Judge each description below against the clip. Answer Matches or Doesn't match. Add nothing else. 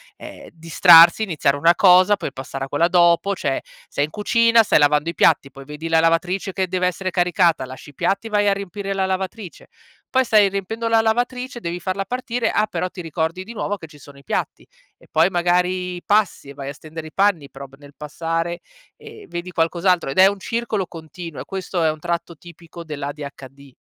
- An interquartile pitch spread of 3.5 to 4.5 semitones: Matches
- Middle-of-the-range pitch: Matches